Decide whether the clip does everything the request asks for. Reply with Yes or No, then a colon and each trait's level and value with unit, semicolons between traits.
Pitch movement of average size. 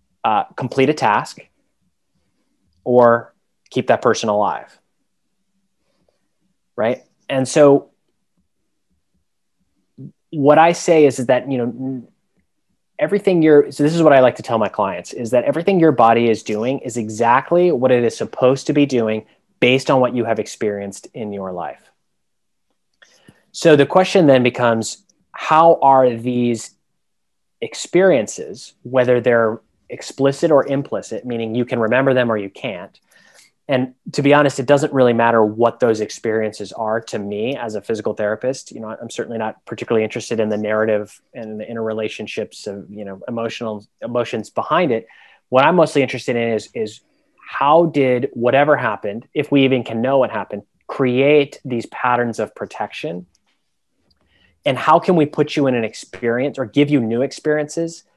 Yes: average, 4.0 semitones